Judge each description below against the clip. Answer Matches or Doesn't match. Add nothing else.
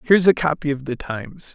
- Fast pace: Matches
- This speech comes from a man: Matches